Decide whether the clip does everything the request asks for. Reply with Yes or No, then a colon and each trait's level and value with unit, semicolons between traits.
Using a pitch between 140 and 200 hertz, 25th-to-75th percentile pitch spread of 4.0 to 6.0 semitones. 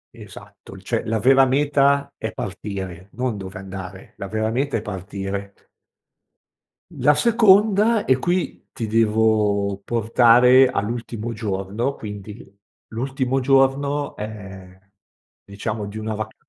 No: low, 110 Hz; average, 5.0 semitones